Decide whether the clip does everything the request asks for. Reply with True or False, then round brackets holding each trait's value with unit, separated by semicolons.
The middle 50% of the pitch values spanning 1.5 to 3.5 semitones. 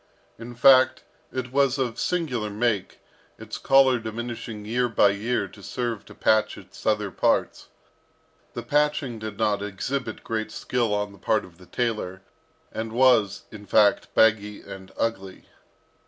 True (3.2 semitones)